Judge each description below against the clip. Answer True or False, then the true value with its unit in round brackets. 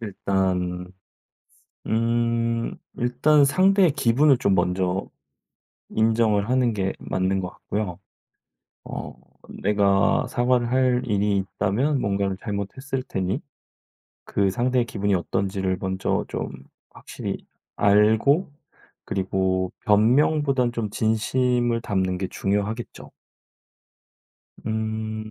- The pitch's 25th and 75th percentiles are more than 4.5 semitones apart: False (4.0 semitones)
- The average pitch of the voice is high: False (110 Hz)